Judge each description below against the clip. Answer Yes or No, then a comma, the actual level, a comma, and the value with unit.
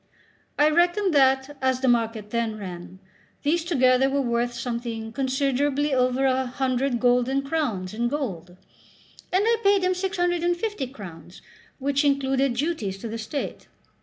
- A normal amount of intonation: Yes, average, 3.8 semitones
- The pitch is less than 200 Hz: No, very high, 265 Hz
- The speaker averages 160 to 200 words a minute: No, average, 140 wpm